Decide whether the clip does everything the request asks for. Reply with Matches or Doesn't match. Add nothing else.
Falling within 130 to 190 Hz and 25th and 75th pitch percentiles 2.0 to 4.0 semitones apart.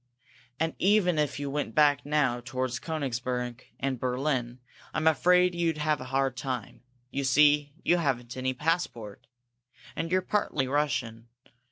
Matches